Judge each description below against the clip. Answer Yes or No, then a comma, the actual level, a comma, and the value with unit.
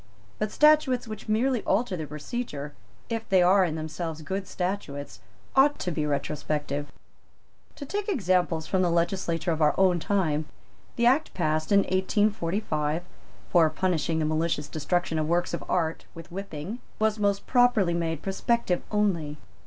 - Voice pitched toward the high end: No, medium, 180 Hz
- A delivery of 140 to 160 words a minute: Yes, average, 155 wpm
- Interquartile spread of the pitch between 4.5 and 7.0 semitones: Yes, average, 4.9 semitones